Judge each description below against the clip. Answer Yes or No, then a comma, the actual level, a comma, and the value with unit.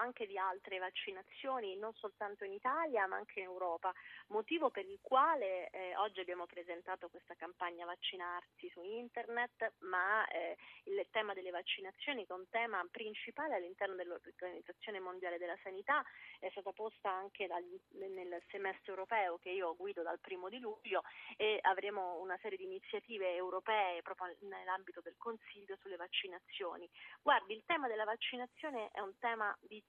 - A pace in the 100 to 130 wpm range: No, average, 155 wpm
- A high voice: Yes, high, 195 Hz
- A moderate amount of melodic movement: Yes, average, 3.7 semitones